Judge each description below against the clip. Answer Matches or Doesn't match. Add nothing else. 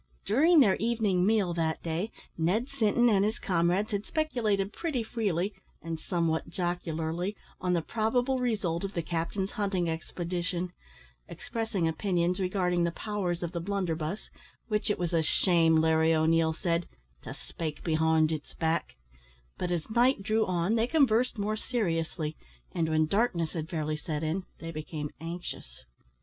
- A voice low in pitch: Doesn't match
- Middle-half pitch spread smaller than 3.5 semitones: Doesn't match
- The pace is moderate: Matches